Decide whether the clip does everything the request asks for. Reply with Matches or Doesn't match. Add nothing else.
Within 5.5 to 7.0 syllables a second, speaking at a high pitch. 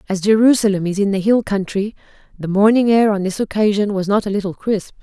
Matches